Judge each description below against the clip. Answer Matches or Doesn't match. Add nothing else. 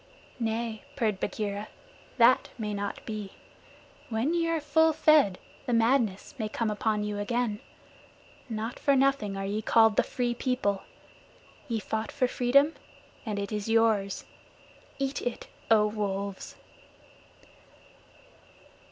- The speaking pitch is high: Matches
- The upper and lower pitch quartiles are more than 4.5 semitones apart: Doesn't match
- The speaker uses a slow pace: Matches